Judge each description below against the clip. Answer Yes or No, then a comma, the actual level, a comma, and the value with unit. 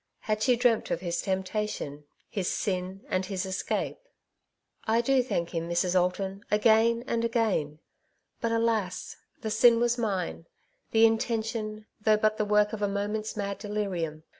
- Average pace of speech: Yes, average, 165 wpm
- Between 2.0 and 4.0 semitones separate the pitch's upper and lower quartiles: Yes, average, 3.2 semitones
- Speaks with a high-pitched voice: Yes, high, 210 Hz